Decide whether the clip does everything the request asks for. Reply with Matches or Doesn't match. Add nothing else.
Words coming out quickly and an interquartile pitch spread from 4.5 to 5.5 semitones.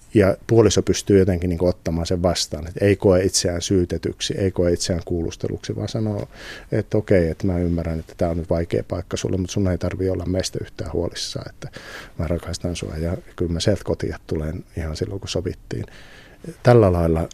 Doesn't match